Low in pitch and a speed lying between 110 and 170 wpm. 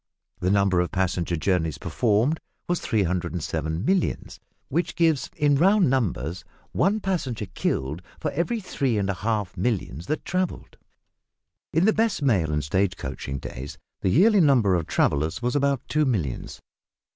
Yes: low, 105 Hz; average, 150 wpm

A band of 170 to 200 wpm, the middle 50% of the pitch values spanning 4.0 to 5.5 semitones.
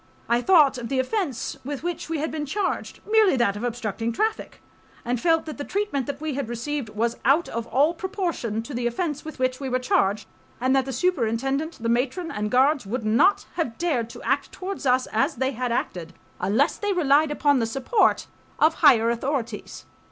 Yes: average, 195 wpm; average, 5.1 semitones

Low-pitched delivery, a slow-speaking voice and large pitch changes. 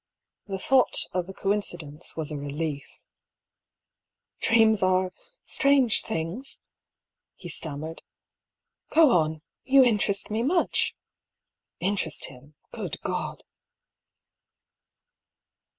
No: medium, 185 Hz; slow, 105 wpm; wide, 6.1 semitones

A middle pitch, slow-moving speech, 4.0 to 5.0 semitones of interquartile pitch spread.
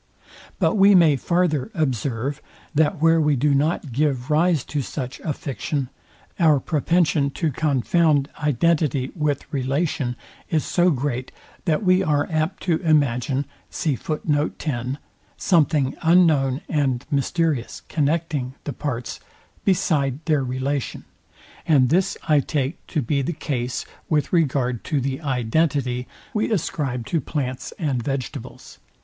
No: medium, 145 Hz; slow, 125 wpm; average, 3.5 semitones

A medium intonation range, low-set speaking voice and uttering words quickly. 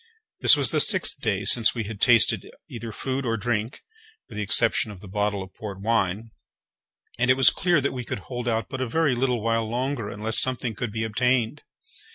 Yes: average, 3.2 semitones; low, 115 Hz; fast, 210 wpm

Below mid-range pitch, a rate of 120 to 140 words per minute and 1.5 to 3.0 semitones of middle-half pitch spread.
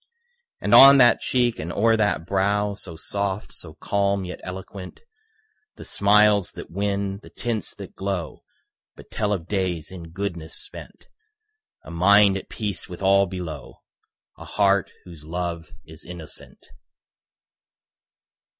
Yes: very low, 95 Hz; slow, 135 wpm; average, 2.7 semitones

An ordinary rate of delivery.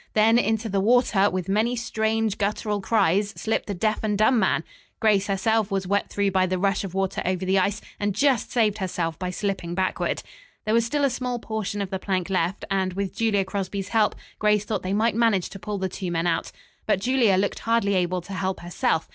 No: fast, 215 wpm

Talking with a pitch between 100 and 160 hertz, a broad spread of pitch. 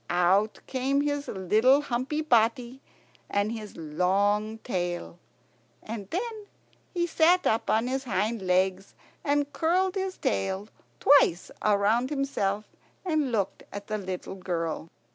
No: high, 220 Hz; wide, 6.7 semitones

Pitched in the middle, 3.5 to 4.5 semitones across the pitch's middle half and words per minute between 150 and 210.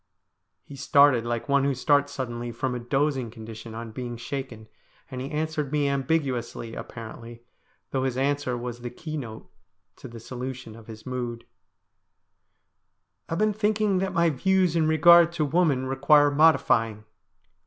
No: low, 130 Hz; average, 4.2 semitones; average, 155 wpm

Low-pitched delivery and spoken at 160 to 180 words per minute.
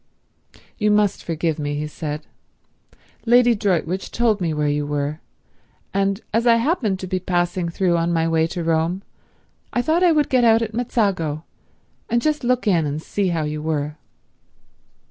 No: medium, 185 Hz; average, 170 wpm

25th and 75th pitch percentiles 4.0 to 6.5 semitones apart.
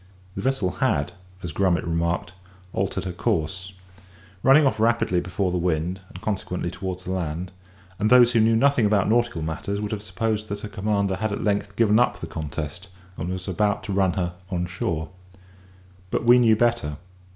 No: average, 3.6 semitones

